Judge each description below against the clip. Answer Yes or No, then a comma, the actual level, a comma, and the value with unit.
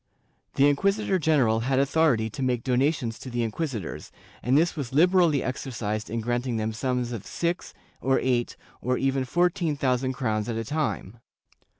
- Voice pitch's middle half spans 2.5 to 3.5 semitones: No, average, 4.1 semitones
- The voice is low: Yes, low, 130 Hz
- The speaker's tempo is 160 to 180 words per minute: Yes, average, 165 wpm